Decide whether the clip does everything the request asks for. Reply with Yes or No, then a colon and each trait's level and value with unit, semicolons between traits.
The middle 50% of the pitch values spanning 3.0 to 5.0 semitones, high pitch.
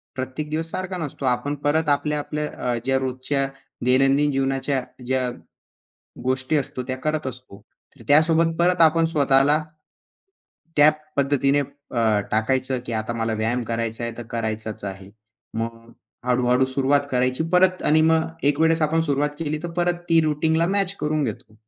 No: average, 3.7 semitones; low, 135 Hz